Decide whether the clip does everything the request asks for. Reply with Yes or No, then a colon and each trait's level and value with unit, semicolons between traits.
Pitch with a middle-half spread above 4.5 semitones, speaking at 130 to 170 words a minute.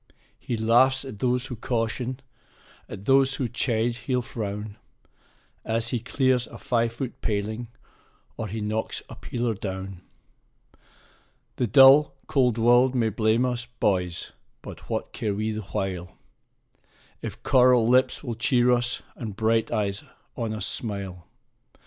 No: average, 2.7 semitones; average, 140 wpm